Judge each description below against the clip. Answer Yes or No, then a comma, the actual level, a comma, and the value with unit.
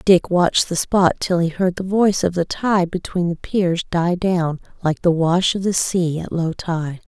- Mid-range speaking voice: Yes, medium, 175 Hz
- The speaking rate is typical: No, fast, 220 wpm